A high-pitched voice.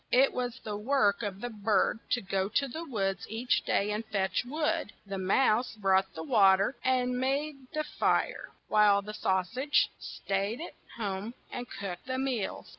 Yes: high, 215 Hz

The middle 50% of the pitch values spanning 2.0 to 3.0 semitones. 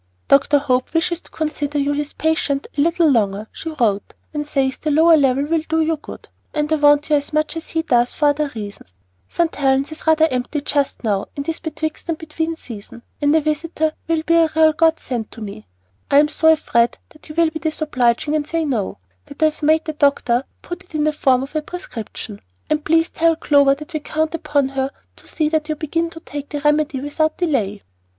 Yes: narrow, 2.6 semitones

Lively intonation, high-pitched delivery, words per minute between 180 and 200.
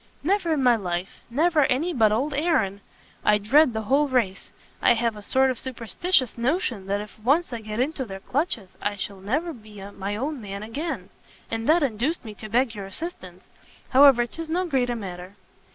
Yes: wide, 6.0 semitones; high, 240 Hz; average, 190 wpm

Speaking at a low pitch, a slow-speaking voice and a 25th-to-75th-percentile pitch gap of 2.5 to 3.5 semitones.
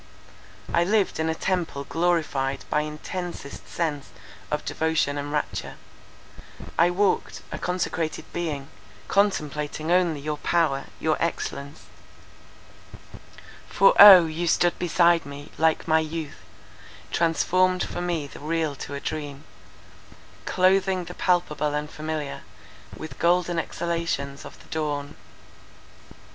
No: medium, 160 Hz; slow, 120 wpm; average, 3.0 semitones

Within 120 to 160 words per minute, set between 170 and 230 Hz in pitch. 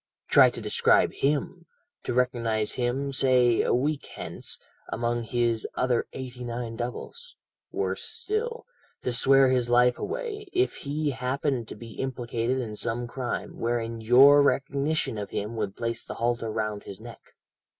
No: average, 150 wpm; low, 125 Hz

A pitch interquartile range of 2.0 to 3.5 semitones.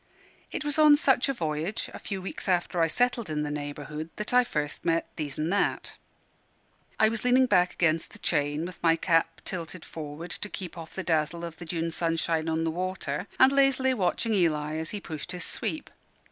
No: average, 4.7 semitones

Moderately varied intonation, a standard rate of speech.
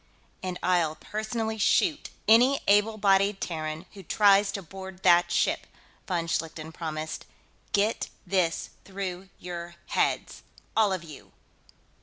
No: average, 3.3 semitones; slow, 125 wpm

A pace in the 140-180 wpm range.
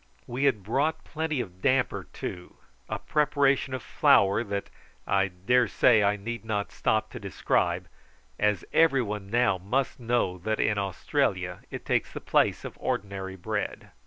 Yes: average, 160 wpm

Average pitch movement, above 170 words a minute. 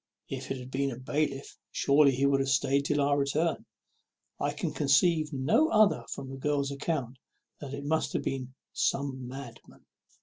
No: narrow, 1.7 semitones; average, 180 wpm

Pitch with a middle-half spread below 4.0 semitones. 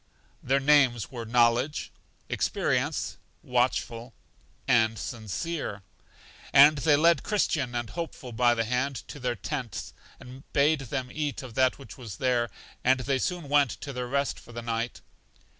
Yes: average, 3.0 semitones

